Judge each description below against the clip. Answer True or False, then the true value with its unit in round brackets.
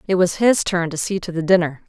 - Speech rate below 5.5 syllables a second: False (5.9 syllables/s)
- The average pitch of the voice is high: False (180 Hz)